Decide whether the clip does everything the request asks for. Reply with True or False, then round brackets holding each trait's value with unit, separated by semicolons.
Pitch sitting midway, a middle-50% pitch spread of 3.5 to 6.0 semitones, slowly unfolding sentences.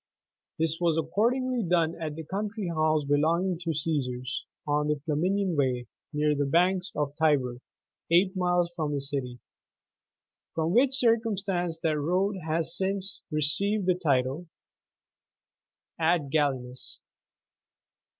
True (165 Hz; 4.0 semitones; 130 wpm)